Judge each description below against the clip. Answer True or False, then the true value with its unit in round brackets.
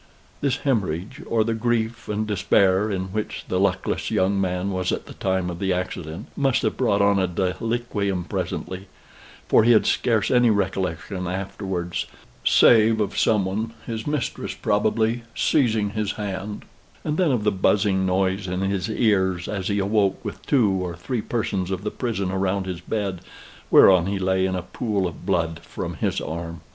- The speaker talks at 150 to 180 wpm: True (175 wpm)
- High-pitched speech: False (100 Hz)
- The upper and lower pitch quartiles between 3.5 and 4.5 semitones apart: False (2.9 semitones)